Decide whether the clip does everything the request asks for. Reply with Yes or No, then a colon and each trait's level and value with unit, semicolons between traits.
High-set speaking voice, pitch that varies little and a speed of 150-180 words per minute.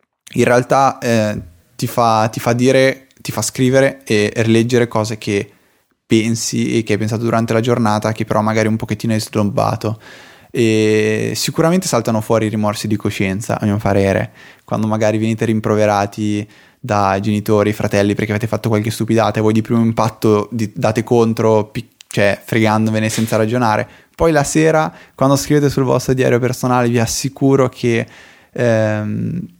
No: low, 110 Hz; narrow, 2.3 semitones; average, 155 wpm